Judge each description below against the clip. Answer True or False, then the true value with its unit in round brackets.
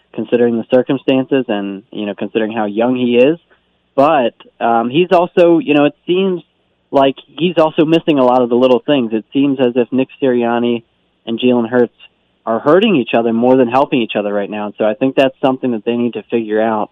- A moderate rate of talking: False (215 wpm)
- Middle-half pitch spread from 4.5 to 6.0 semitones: False (3.4 semitones)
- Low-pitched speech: True (125 Hz)